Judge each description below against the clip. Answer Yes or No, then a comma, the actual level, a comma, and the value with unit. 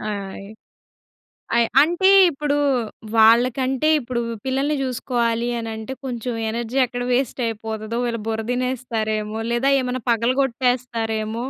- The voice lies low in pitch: No, high, 240 Hz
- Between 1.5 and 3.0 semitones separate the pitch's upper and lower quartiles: Yes, narrow, 2.5 semitones